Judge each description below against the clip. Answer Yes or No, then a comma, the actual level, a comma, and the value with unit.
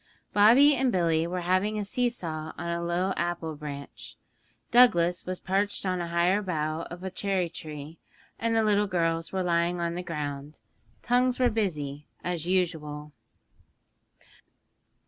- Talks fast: No, average, 150 wpm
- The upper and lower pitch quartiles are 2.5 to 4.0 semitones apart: Yes, average, 3.6 semitones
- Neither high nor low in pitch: Yes, medium, 175 Hz